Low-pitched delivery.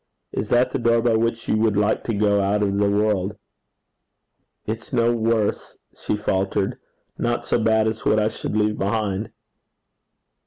Yes: low, 110 Hz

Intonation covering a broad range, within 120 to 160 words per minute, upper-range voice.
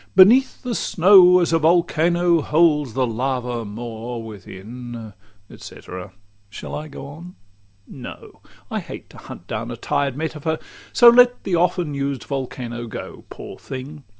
No: wide, 6.3 semitones; average, 150 wpm; medium, 140 Hz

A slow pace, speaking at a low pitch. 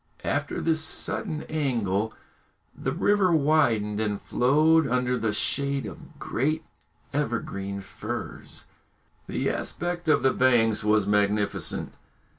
Yes: slow, 110 wpm; low, 125 Hz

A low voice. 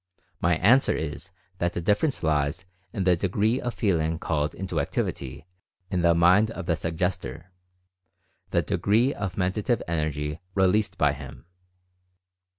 Yes: very low, 85 Hz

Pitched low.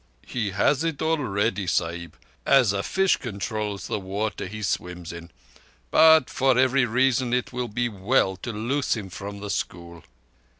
Yes: low, 110 Hz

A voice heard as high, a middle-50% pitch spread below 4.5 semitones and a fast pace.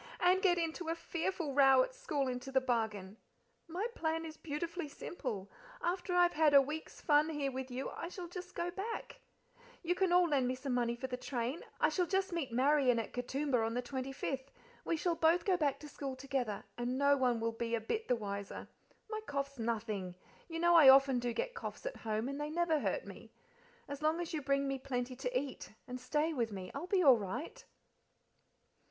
No: very high, 280 Hz; average, 5.2 semitones; fast, 210 wpm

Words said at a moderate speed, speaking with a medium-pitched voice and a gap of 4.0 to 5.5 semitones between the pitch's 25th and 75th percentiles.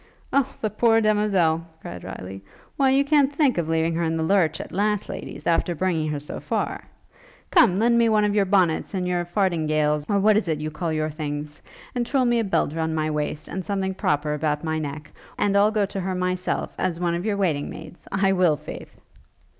No: fast, 215 wpm; medium, 180 Hz; average, 4.9 semitones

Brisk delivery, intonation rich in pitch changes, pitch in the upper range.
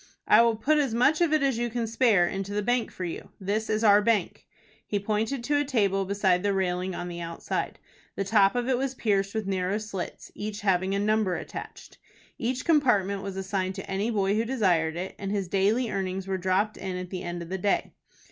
No: fast, 225 wpm; average, 3.2 semitones; high, 200 Hz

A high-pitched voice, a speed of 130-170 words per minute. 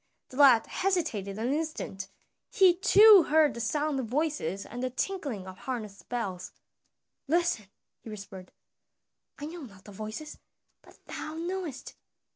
Yes: very high, 265 Hz; average, 140 wpm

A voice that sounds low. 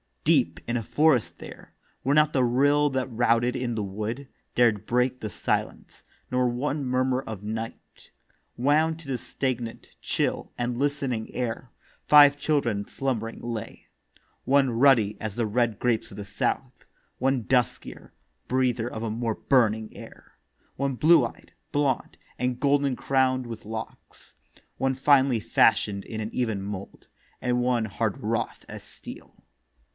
Yes: low, 125 Hz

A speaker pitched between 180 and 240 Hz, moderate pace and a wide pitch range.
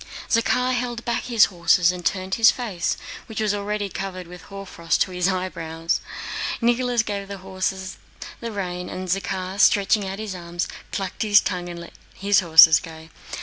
No: high, 190 Hz; average, 170 wpm; average, 2.8 semitones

